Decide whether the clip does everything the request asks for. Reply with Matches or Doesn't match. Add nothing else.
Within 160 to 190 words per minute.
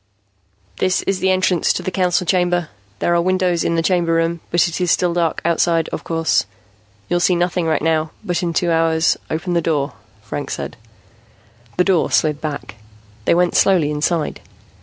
Matches